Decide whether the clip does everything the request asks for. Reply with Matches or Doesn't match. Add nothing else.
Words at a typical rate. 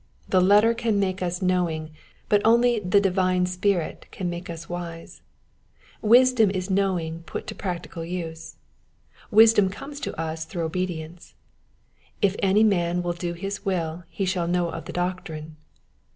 Matches